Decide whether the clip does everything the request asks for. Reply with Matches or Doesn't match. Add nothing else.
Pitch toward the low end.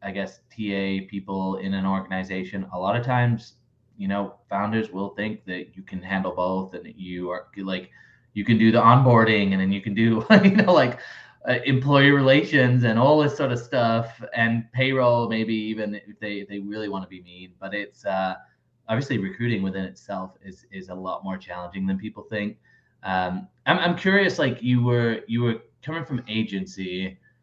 Matches